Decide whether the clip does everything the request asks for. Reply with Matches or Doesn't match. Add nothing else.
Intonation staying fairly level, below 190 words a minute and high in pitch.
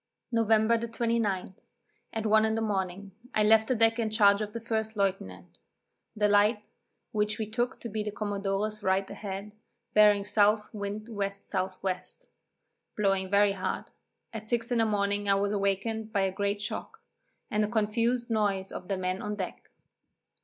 Matches